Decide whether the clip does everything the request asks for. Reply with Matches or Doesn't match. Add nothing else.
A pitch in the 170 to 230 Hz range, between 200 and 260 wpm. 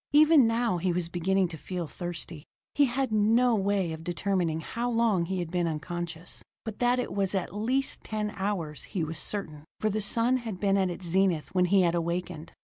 Matches